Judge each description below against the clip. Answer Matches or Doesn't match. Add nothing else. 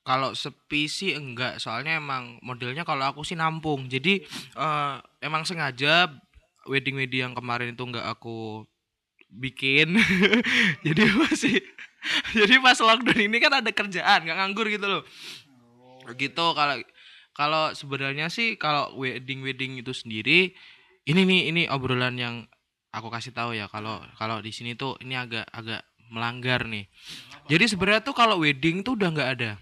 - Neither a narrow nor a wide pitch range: Doesn't match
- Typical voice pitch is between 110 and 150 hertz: Matches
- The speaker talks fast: Matches